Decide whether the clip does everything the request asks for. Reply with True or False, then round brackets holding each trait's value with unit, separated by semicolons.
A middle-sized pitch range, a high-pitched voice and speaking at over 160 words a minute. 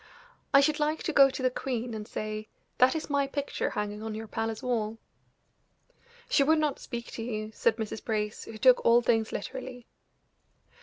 True (3.9 semitones; 235 Hz; 185 wpm)